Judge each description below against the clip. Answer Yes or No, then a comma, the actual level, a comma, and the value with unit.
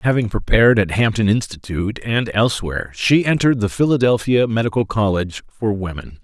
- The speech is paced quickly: No, average, 145 wpm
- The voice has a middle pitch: No, low, 110 Hz